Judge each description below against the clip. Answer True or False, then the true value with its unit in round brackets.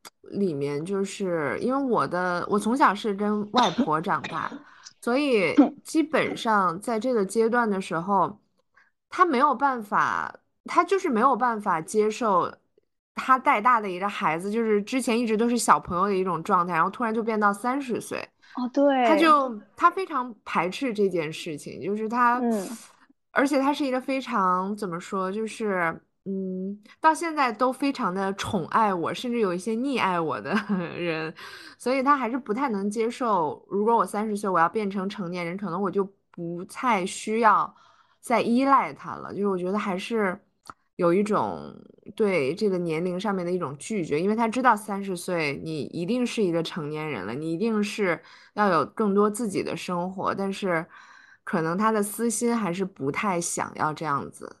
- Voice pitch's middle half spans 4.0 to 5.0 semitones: True (4.6 semitones)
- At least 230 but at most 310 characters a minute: True (255 characters per minute)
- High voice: True (210 Hz)